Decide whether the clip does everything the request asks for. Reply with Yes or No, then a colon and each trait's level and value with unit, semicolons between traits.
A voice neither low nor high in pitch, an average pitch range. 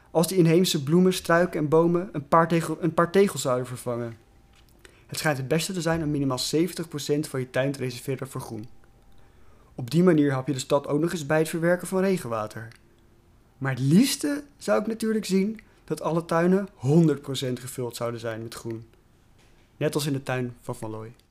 No: medium, 145 Hz; wide, 5.9 semitones